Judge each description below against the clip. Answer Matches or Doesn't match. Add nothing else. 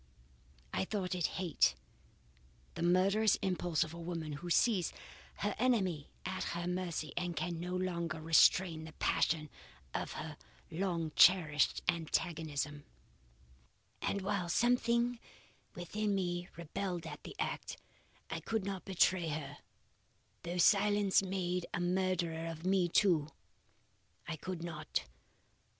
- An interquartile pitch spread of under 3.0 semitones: Matches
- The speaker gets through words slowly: Matches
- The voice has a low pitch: Doesn't match